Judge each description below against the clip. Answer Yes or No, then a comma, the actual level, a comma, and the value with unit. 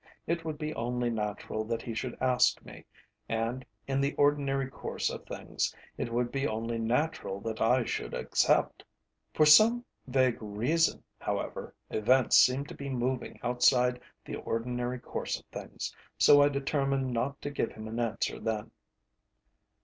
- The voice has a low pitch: Yes, low, 125 Hz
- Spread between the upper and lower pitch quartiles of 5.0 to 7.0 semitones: No, average, 3.2 semitones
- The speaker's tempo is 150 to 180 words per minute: Yes, average, 155 wpm